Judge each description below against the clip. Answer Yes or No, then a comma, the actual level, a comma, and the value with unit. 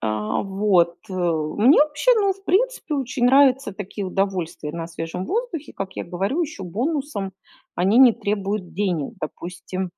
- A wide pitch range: Yes, wide, 7.5 semitones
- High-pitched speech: Yes, high, 200 Hz